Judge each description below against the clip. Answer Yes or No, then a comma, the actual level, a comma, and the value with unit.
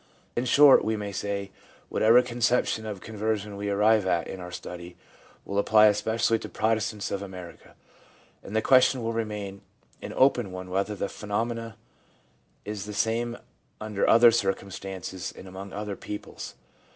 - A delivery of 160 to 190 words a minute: No, average, 150 wpm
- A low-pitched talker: Yes, low, 105 Hz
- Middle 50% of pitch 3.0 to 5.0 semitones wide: No, narrow, 2.5 semitones